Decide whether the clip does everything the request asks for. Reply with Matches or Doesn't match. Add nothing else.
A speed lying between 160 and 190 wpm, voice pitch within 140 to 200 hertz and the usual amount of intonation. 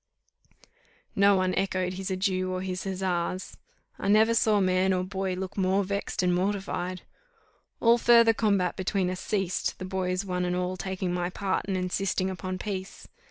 Doesn't match